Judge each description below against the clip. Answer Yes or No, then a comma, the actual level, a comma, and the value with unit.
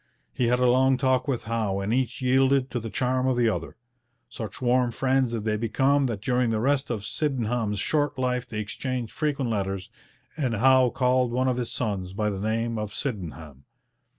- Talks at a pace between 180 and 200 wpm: Yes, average, 195 wpm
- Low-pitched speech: Yes, low, 120 Hz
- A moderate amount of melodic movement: Yes, average, 3.2 semitones